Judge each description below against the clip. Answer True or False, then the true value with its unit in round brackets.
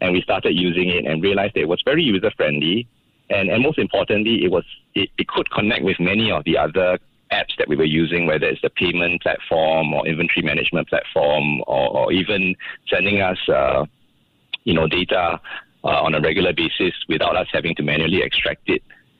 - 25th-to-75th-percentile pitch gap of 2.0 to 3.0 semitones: True (2.6 semitones)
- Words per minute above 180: True (195 wpm)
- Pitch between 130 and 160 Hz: False (90 Hz)